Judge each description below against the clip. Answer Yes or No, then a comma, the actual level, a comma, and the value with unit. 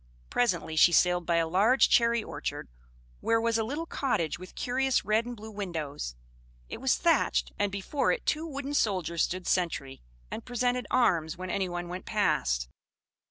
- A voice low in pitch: No, high, 205 Hz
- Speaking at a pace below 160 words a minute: No, average, 165 wpm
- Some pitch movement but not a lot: No, wide, 6.0 semitones